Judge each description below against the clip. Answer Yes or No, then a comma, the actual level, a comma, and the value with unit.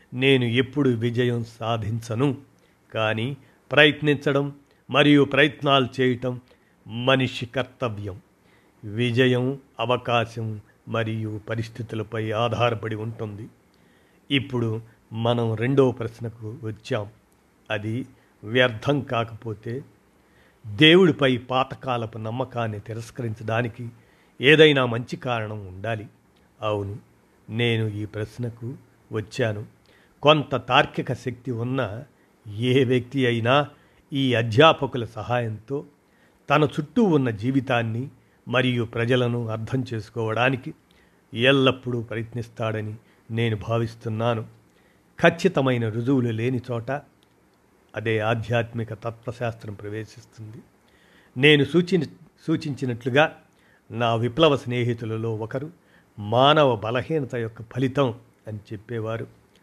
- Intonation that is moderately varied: Yes, average, 3.0 semitones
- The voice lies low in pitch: Yes, low, 120 Hz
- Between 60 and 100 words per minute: Yes, average, 80 wpm